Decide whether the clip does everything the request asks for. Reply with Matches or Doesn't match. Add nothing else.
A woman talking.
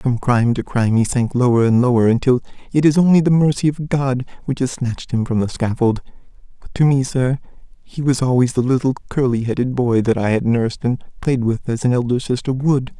Doesn't match